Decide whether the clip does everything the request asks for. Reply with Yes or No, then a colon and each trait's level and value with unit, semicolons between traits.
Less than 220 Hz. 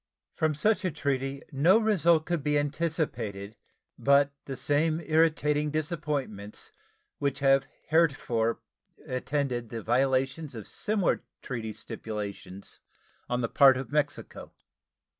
Yes: medium, 140 Hz